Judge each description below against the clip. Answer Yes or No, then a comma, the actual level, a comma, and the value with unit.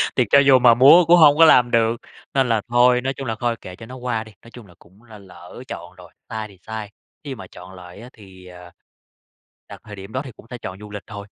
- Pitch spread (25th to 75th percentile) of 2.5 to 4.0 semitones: No, average, 4.5 semitones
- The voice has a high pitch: No, low, 115 Hz